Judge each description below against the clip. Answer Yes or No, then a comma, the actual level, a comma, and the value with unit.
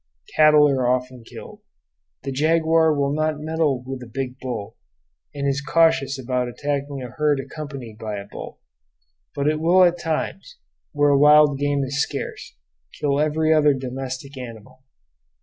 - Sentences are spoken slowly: No, average, 150 wpm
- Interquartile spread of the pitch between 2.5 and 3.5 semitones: Yes, average, 2.9 semitones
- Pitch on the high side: No, medium, 140 Hz